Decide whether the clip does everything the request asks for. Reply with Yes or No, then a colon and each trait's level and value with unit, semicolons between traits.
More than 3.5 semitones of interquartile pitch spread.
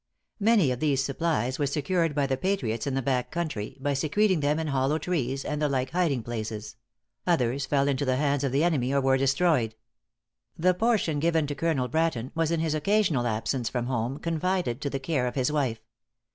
Yes: average, 4.0 semitones